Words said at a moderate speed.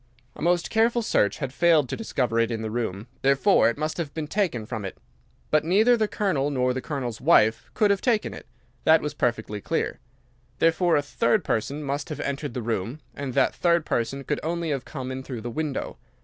No: fast, 210 wpm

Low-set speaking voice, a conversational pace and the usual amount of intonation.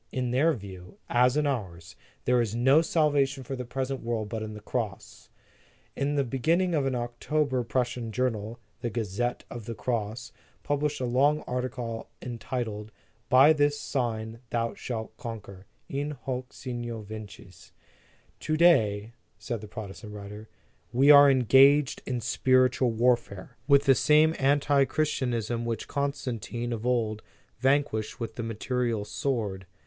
Yes: low, 120 Hz; average, 145 wpm; average, 3.7 semitones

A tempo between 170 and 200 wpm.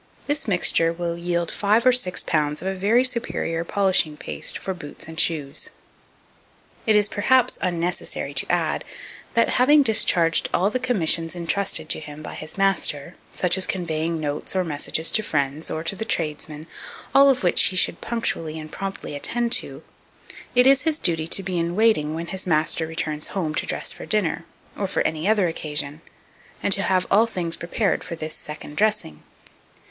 Yes: average, 180 wpm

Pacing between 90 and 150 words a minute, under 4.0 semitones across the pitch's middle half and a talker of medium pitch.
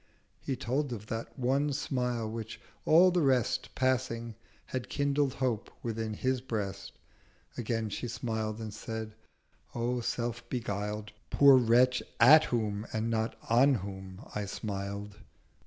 No: average, 140 wpm; average, 3.0 semitones; low, 115 Hz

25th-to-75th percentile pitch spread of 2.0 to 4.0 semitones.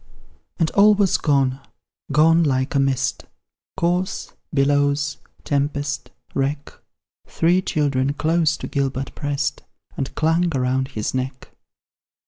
Yes: average, 3.0 semitones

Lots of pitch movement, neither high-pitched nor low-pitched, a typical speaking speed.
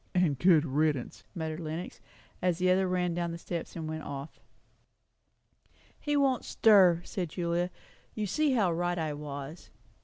No: average, 2.7 semitones; medium, 170 Hz; average, 160 wpm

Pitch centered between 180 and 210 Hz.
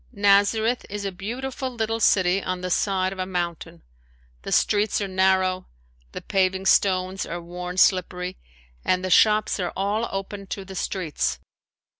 Yes: high, 190 Hz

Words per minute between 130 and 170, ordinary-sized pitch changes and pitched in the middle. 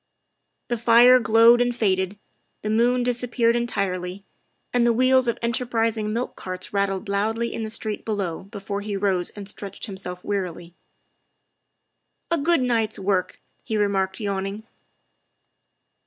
No: average, 140 wpm; average, 3.2 semitones; high, 215 Hz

